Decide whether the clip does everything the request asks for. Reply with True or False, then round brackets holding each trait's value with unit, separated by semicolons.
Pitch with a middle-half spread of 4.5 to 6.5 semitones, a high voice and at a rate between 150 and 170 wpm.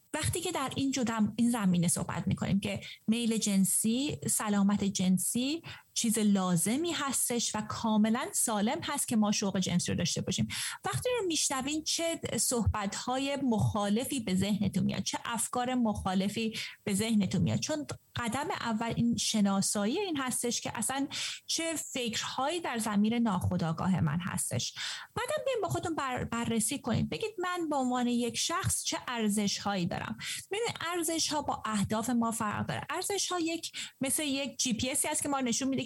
True (5.3 semitones; 235 Hz; 155 wpm)